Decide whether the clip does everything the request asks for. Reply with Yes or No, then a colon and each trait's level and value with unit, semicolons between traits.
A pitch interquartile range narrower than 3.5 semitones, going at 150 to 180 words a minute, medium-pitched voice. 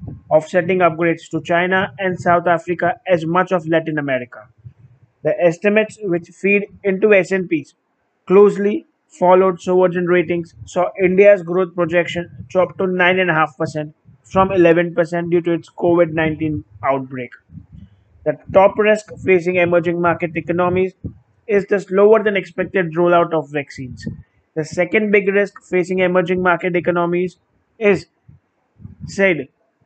No: average, 2.8 semitones; average, 140 wpm; medium, 175 Hz